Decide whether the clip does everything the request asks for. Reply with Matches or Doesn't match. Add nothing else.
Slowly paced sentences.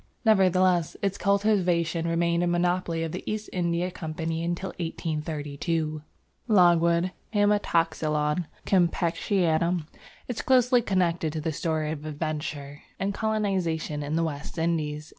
Matches